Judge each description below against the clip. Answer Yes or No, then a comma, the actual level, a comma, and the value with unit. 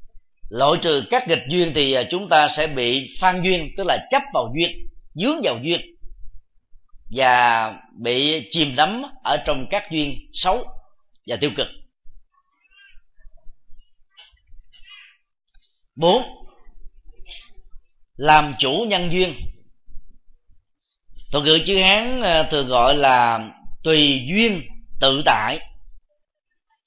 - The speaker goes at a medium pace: No, slow, 105 wpm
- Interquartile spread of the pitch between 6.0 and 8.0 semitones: Yes, wide, 6.6 semitones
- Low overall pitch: No, medium, 155 Hz